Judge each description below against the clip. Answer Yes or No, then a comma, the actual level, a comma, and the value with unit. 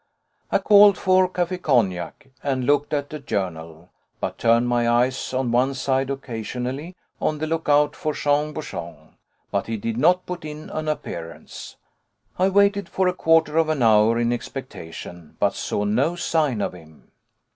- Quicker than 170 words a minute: No, average, 165 wpm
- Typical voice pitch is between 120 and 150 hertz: Yes, low, 135 Hz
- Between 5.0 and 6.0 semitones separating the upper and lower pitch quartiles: Yes, wide, 5.5 semitones